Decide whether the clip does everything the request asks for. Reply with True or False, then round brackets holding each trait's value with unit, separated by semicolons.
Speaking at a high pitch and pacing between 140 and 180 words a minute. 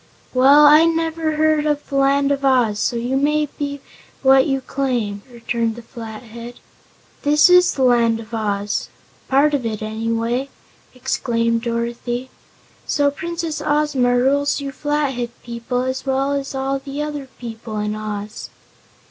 True (265 Hz; 150 wpm)